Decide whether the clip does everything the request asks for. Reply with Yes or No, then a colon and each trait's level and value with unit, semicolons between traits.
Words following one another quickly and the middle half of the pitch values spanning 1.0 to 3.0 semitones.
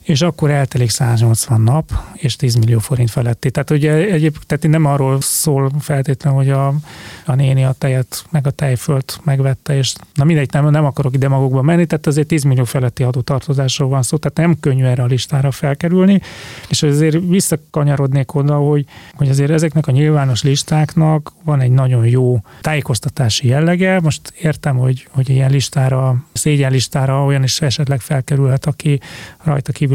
Yes: fast, 165 wpm; narrow, 2.5 semitones